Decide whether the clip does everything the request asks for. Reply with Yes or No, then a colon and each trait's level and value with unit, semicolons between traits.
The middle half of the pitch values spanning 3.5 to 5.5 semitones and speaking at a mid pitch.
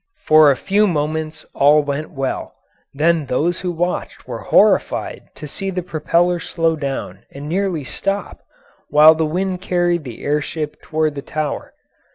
No: average, 2.9 semitones; medium, 155 Hz